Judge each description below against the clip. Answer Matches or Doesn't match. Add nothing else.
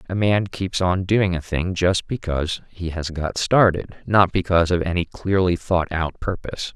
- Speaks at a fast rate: Doesn't match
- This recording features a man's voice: Matches